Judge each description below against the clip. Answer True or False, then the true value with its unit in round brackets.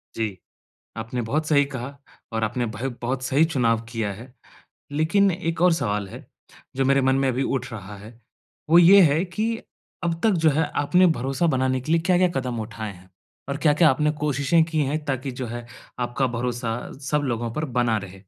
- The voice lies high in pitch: False (135 Hz)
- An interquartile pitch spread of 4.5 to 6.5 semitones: True (5.1 semitones)